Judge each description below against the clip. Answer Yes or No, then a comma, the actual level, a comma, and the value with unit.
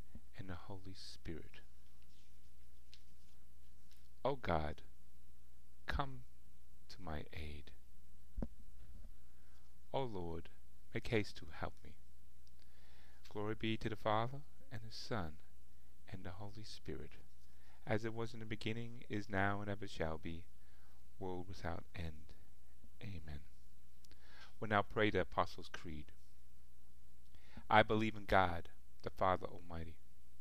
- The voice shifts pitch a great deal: Yes, wide, 7.7 semitones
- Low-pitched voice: Yes, very low, 65 Hz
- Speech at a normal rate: No, slow, 115 wpm